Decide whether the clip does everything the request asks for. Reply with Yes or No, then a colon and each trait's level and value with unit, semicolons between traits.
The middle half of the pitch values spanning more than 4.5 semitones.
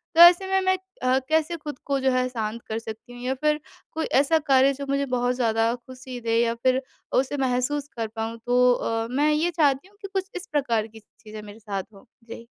No: average, 4.2 semitones